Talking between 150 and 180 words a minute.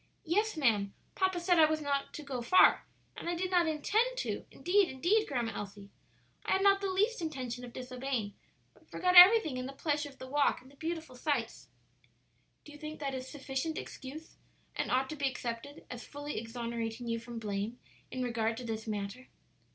No: average, 195 wpm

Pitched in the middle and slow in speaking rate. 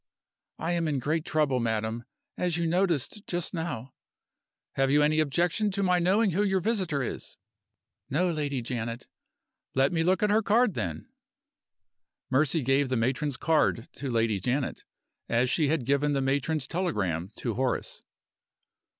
No: medium, 145 Hz; average, 160 wpm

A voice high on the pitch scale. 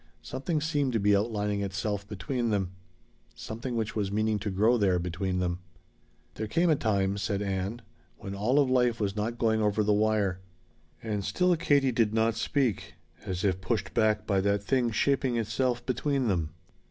No: low, 110 Hz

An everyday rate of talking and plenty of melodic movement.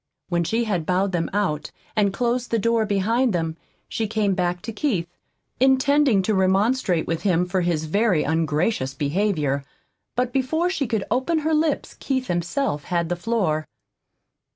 Yes: average, 160 wpm; wide, 5.8 semitones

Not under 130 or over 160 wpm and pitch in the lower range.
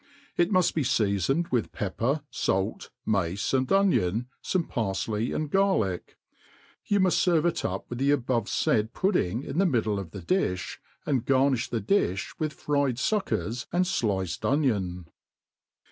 Yes: average, 145 wpm; low, 125 Hz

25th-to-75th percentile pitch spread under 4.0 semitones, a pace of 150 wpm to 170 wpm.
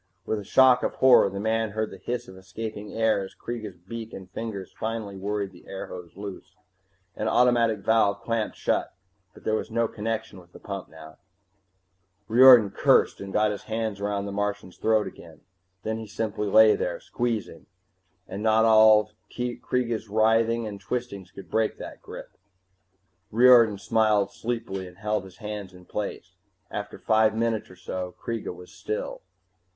Yes: narrow, 2.5 semitones; average, 165 wpm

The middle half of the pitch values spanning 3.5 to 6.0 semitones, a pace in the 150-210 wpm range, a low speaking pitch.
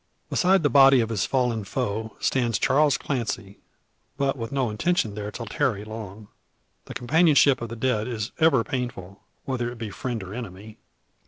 Yes: average, 4.0 semitones; average, 170 wpm; low, 115 Hz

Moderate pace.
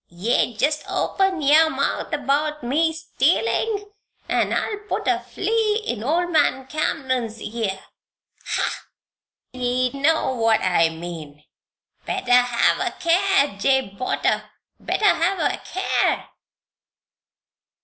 No: slow, 115 wpm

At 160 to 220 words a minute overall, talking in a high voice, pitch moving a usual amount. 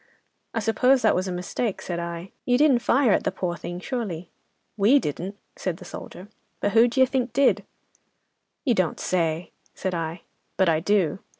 No: average, 180 wpm; high, 195 Hz; wide, 5.8 semitones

